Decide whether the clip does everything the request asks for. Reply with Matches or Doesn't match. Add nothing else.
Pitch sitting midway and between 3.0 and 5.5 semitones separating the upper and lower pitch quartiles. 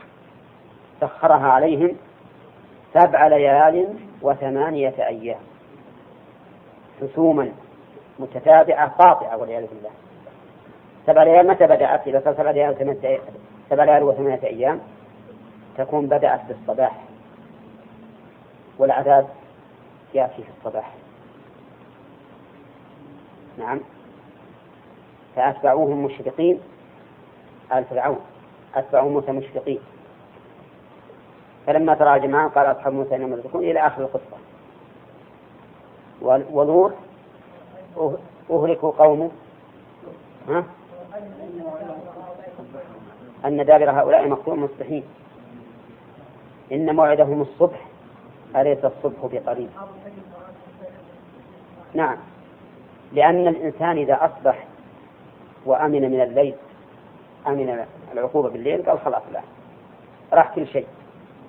Matches